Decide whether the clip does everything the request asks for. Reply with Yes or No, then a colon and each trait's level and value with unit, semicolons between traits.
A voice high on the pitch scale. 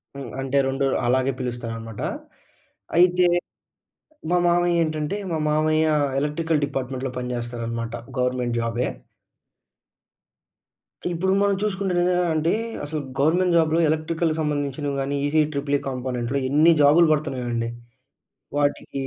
No: medium, 145 Hz